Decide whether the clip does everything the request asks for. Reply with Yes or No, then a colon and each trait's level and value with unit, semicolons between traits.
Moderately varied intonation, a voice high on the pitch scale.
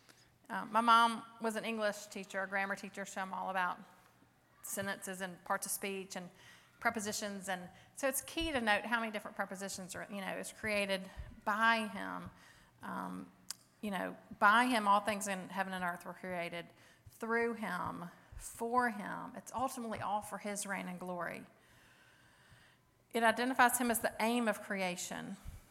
Yes: average, 3.0 semitones; high, 205 Hz